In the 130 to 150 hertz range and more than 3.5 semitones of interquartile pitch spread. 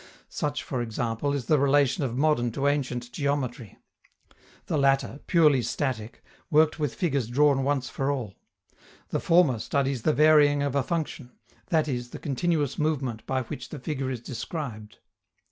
No: medium, 140 Hz; average, 3.2 semitones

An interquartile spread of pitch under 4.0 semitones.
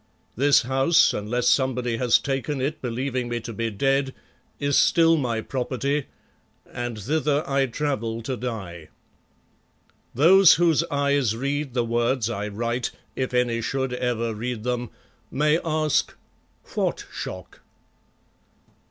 Yes: average, 3.3 semitones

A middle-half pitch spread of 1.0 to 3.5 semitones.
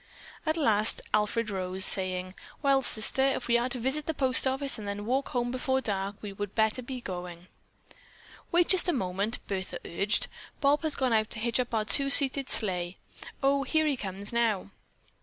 No: average, 5.1 semitones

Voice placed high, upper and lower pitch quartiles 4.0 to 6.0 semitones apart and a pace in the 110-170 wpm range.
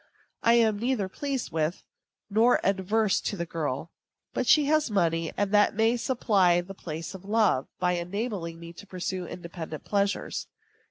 Yes: high, 195 Hz; average, 4.5 semitones; average, 160 wpm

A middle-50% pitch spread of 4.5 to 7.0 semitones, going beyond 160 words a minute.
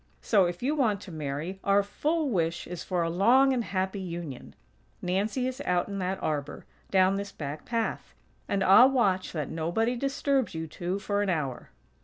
Yes: average, 5.0 semitones; average, 185 wpm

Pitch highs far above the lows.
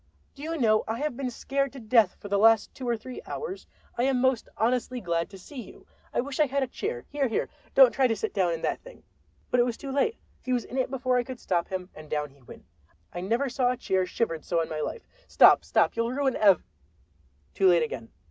Yes: wide, 6.2 semitones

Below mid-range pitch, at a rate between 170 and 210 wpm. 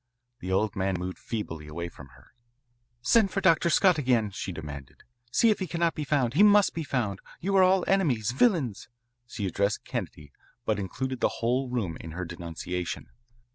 Yes: low, 115 Hz; average, 180 wpm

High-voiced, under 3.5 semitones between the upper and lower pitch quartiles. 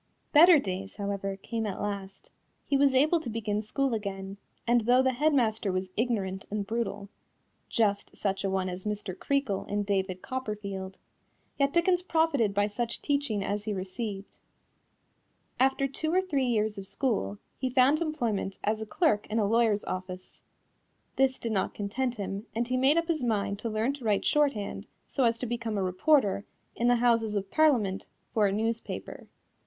No: high, 220 Hz; average, 4.6 semitones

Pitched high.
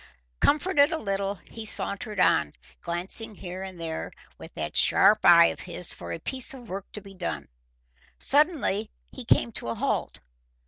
Yes: high, 200 Hz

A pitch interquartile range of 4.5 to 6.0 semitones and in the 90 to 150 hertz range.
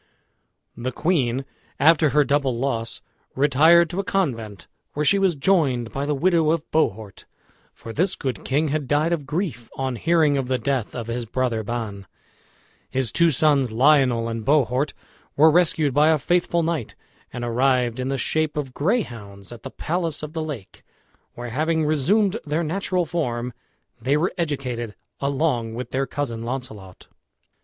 Yes: average, 4.8 semitones; medium, 140 Hz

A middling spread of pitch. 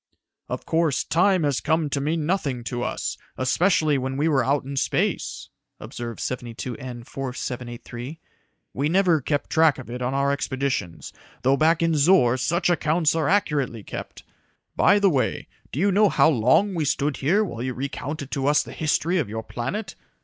Yes: average, 4.4 semitones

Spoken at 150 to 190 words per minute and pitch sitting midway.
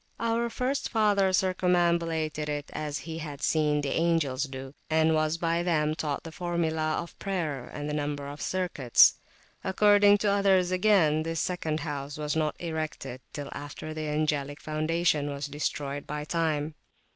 Yes: average, 155 wpm; medium, 155 Hz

